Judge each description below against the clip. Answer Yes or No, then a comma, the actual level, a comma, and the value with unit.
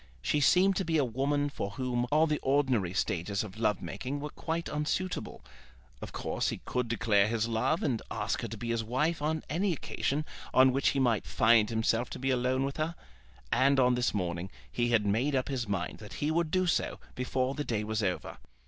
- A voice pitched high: No, low, 125 Hz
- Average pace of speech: No, fast, 210 wpm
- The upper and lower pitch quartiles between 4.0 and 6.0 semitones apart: Yes, average, 4.8 semitones